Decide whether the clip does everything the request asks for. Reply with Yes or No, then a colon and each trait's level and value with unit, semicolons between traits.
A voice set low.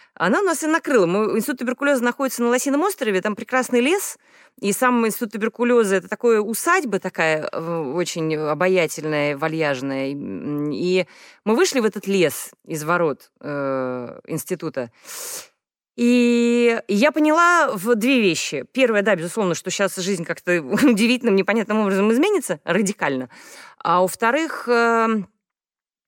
No: high, 215 Hz